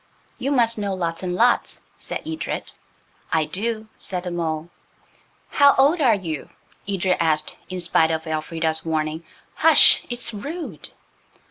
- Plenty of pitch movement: Yes, wide, 6.6 semitones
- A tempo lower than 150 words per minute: Yes, average, 140 wpm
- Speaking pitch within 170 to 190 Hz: Yes, medium, 185 Hz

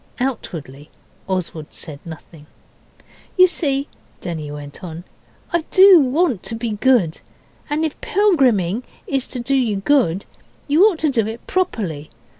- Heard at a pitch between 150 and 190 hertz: No, high, 235 Hz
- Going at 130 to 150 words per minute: Yes, average, 140 wpm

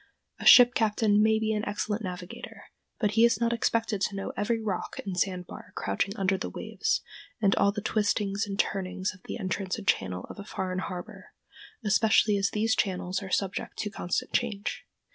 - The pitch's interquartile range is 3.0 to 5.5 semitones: No, narrow, 2.4 semitones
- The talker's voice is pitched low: No, high, 200 Hz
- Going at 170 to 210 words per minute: Yes, average, 185 wpm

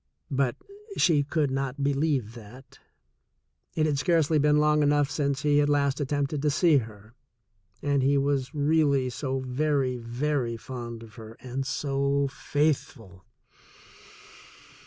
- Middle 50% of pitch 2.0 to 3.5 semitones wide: Yes, narrow, 2.5 semitones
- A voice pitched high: No, medium, 140 Hz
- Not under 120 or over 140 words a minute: Yes, slow, 135 wpm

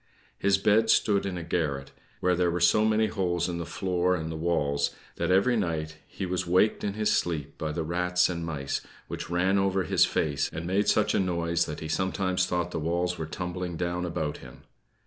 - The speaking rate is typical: No, fast, 210 wpm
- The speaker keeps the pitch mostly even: Yes, narrow, 2.3 semitones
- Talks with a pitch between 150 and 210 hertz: No, very low, 90 Hz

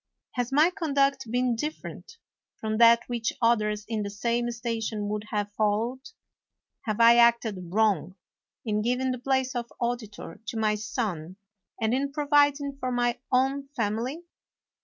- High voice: Yes, high, 235 Hz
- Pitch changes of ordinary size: Yes, average, 3.4 semitones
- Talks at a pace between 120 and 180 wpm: Yes, average, 145 wpm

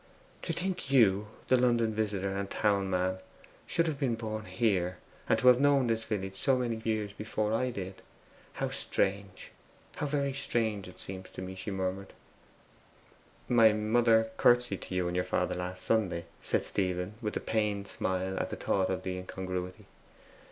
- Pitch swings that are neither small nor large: Yes, average, 3.8 semitones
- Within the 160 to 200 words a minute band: Yes, average, 170 wpm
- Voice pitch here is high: No, low, 105 Hz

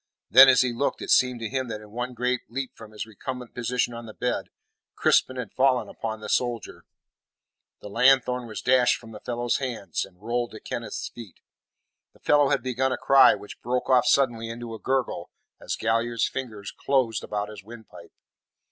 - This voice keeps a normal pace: Yes, average, 190 wpm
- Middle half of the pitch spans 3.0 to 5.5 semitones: No, narrow, 2.4 semitones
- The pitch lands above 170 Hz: No, low, 120 Hz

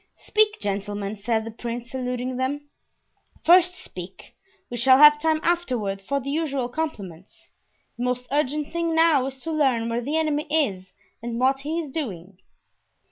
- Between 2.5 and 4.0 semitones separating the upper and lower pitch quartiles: No, average, 5.0 semitones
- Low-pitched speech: No, very high, 260 Hz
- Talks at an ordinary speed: Yes, average, 160 wpm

